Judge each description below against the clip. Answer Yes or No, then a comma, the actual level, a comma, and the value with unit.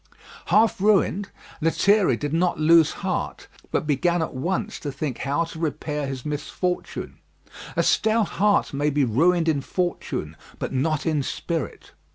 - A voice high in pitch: No, medium, 160 Hz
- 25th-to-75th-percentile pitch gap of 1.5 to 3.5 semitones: No, average, 3.9 semitones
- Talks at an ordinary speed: Yes, average, 150 wpm